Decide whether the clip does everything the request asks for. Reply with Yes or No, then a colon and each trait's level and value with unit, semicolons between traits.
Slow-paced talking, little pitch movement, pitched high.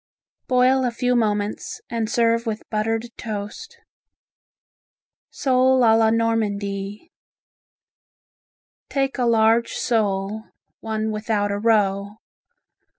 Yes: slow, 95 wpm; narrow, 2.2 semitones; high, 225 Hz